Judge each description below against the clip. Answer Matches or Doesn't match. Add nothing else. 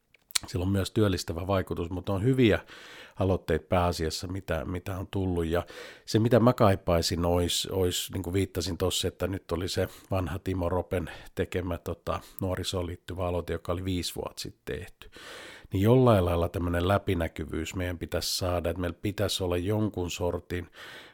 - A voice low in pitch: Matches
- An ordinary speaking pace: Doesn't match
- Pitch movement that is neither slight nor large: Doesn't match